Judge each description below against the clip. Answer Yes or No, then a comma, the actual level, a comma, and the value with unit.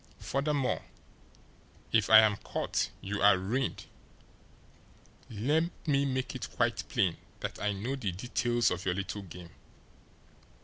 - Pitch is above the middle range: No, low, 110 Hz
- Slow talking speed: Yes, slow, 130 wpm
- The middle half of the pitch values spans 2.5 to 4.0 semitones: No, average, 5.1 semitones